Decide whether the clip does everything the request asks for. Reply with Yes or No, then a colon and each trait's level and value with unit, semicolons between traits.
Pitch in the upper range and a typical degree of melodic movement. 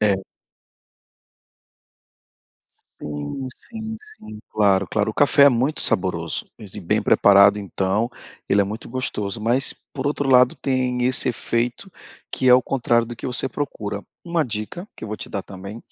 No: low, 115 Hz; average, 4.4 semitones